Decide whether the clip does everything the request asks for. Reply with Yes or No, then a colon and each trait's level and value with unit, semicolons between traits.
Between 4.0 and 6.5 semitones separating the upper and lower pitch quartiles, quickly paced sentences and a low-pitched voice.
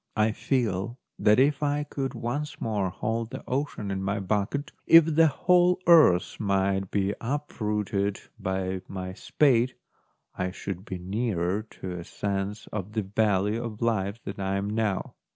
No: average, 4.3 semitones; average, 155 wpm; low, 105 Hz